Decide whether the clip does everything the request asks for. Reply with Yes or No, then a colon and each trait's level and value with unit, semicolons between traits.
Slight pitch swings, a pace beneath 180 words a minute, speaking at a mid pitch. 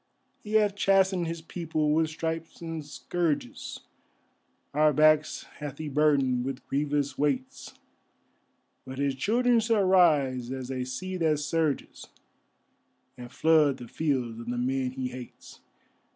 No: average, 3.9 semitones; slow, 135 wpm; medium, 150 Hz